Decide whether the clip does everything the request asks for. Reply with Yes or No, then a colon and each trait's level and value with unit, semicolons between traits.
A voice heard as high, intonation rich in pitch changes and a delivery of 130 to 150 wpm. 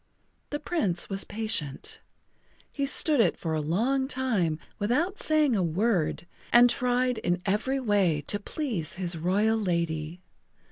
Yes: high, 205 Hz; wide, 6.8 semitones; average, 140 wpm